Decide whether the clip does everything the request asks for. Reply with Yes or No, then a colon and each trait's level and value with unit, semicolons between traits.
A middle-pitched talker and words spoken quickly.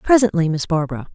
No: medium, 180 Hz; average, 160 wpm